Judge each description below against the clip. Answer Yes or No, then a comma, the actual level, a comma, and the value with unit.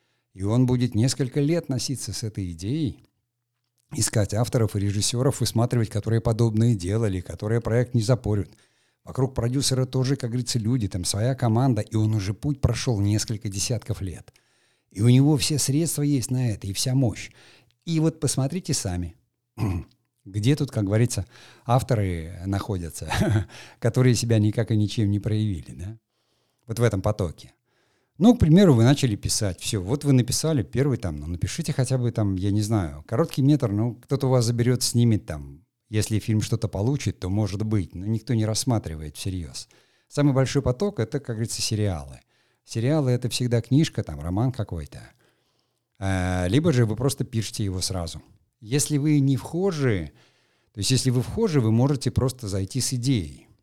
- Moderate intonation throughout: Yes, average, 3.8 semitones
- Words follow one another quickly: Yes, fast, 165 wpm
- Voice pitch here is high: No, low, 115 Hz